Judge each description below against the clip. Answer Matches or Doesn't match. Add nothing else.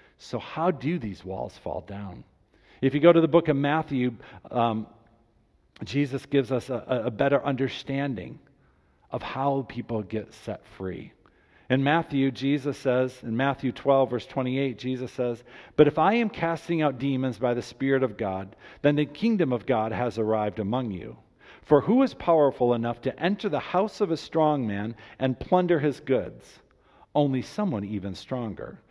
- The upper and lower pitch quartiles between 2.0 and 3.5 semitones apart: Doesn't match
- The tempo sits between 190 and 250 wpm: Doesn't match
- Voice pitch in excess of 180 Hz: Doesn't match